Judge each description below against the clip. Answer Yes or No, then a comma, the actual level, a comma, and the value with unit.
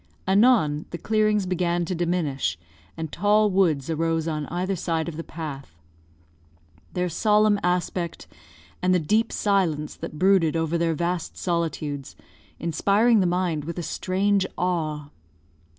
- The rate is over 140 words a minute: No, slow, 135 wpm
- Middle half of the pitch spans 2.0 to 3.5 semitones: Yes, average, 3.1 semitones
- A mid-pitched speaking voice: Yes, medium, 175 Hz